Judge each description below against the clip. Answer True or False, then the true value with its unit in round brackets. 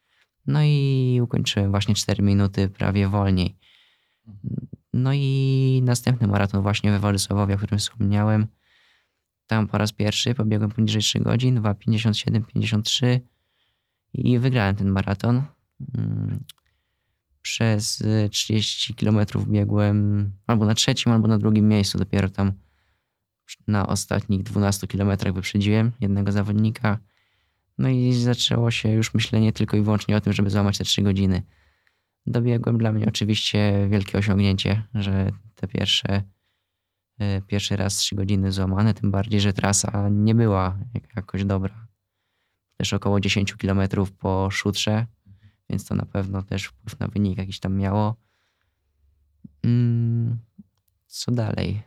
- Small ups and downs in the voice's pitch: True (2.1 semitones)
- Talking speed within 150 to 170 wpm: False (125 wpm)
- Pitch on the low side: True (105 Hz)